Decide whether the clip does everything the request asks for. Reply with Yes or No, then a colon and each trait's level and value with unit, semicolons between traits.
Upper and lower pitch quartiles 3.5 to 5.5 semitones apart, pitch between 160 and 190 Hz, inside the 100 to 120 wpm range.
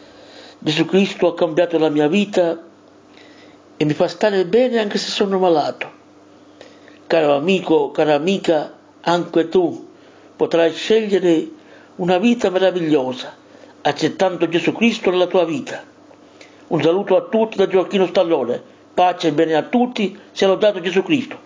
No: average, 4.5 semitones; medium, 185 Hz; average, 135 wpm